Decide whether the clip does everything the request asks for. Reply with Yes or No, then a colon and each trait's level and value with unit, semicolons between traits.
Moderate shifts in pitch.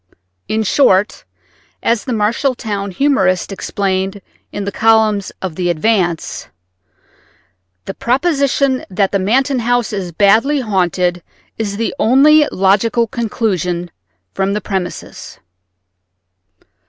Yes: average, 4.0 semitones